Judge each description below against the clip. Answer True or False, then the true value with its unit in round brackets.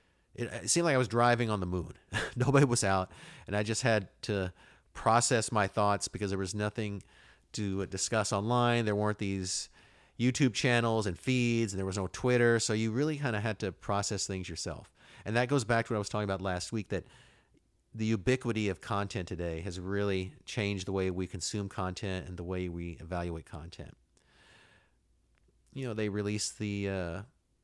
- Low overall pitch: True (105 Hz)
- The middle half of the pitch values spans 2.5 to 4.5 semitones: True (3.5 semitones)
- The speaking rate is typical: True (190 wpm)